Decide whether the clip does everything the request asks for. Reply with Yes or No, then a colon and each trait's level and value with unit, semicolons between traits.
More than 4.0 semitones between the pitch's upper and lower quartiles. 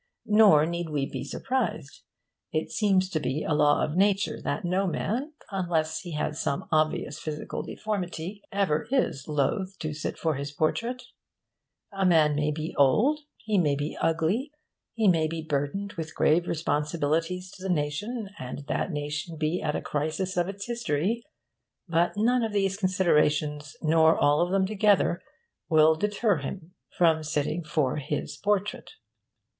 Yes: average, 4.5 semitones